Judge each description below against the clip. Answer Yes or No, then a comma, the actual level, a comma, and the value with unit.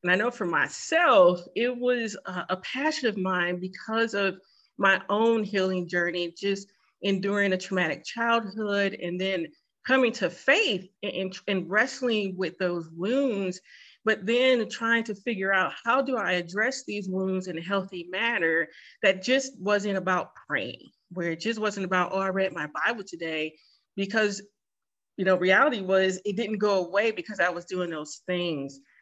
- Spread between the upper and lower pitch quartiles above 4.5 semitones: No, average, 3.4 semitones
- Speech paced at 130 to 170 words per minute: Yes, average, 165 wpm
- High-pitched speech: Yes, high, 195 Hz